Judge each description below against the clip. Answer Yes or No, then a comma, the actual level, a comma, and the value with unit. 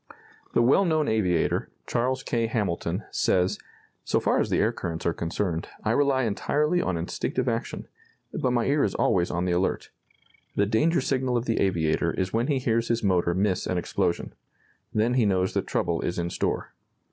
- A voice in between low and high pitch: No, low, 105 Hz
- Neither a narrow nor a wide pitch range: No, wide, 5.9 semitones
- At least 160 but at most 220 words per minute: Yes, average, 185 wpm